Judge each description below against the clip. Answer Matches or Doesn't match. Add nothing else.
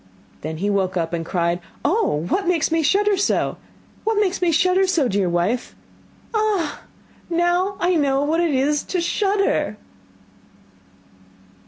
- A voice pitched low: Doesn't match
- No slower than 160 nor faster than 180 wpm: Doesn't match